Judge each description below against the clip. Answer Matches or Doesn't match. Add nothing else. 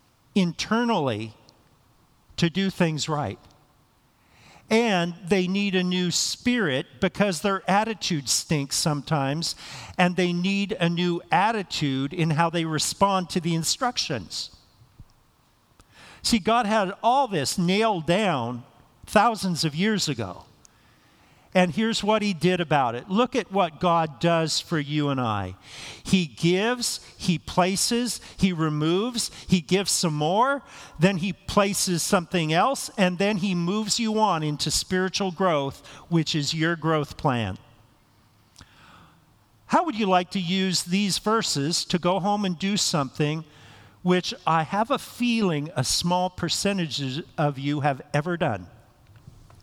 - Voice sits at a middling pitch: Matches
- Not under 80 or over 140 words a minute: Matches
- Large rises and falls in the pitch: Doesn't match